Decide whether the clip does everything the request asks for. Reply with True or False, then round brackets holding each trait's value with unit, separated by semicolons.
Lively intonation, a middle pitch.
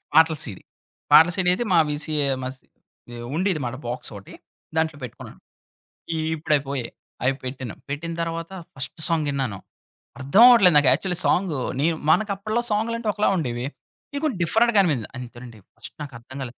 True (6.2 semitones; 155 Hz)